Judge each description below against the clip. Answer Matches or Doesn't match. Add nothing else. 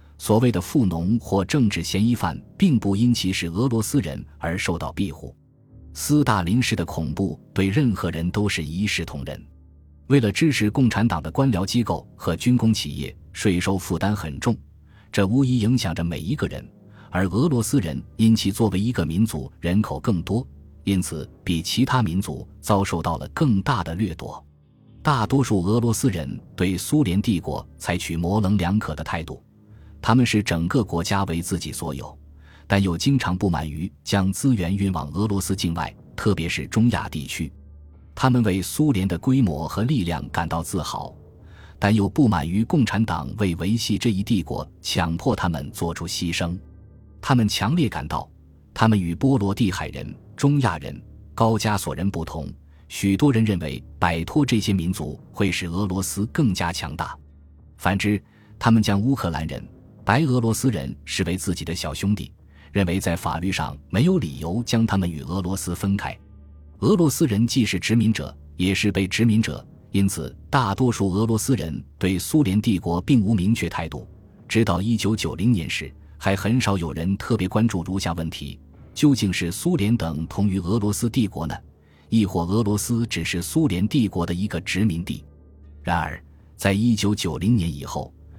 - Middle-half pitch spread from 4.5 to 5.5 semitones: Matches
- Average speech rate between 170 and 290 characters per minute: Matches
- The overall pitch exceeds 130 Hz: Doesn't match